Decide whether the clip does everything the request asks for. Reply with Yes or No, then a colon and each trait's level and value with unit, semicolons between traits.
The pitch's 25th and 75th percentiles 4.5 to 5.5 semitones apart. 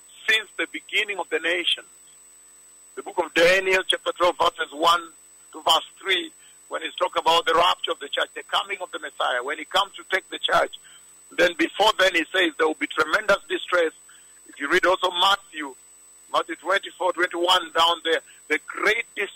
No: average, 2.9 semitones